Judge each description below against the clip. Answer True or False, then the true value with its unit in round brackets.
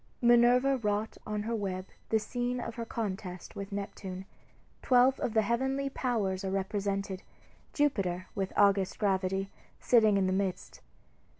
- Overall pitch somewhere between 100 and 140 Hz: False (205 Hz)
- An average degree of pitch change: True (3.7 semitones)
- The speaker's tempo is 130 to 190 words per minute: True (140 wpm)